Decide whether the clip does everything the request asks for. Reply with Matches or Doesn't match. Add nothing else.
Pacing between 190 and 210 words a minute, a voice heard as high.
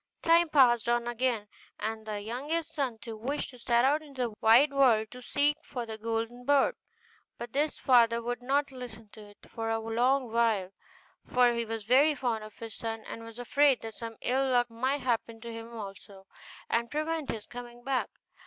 Matches